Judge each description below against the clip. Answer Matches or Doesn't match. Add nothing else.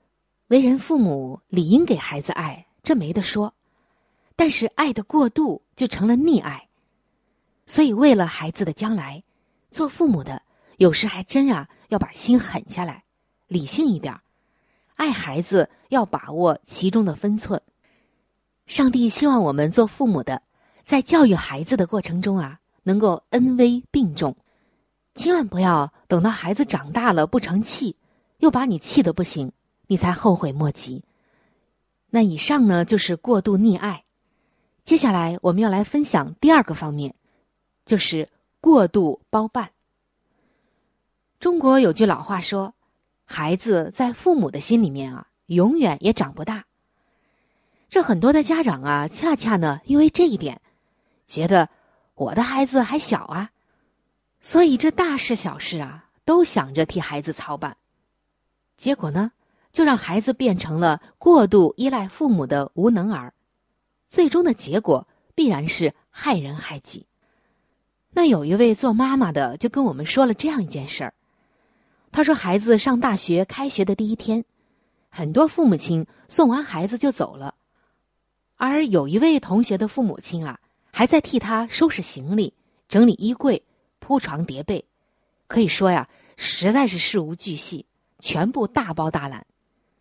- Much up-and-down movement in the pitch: Matches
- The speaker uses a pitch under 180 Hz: Doesn't match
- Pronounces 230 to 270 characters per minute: Doesn't match